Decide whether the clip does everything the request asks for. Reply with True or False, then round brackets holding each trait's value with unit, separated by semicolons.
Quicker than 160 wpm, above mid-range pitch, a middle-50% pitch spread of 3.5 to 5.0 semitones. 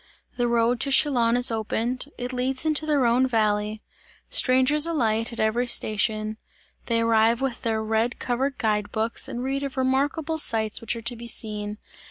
False (175 wpm; 235 Hz; 2.9 semitones)